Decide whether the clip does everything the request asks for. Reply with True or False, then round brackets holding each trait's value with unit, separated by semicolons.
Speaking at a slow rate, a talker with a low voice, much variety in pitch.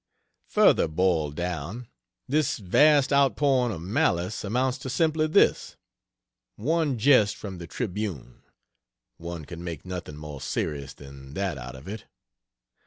True (130 wpm; 95 Hz; 8.2 semitones)